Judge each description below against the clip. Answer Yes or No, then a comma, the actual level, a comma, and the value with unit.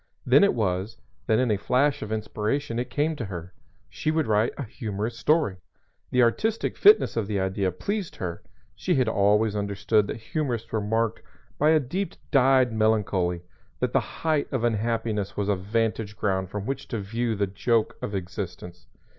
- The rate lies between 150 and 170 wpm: No, average, 180 wpm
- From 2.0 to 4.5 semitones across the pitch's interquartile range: Yes, average, 4.0 semitones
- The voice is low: Yes, low, 110 Hz